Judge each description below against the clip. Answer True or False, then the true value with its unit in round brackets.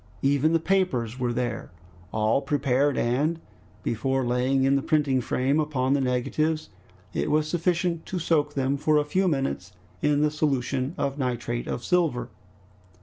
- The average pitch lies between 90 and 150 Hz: True (140 Hz)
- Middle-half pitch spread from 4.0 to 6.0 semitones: False (3.3 semitones)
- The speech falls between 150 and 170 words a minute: True (155 wpm)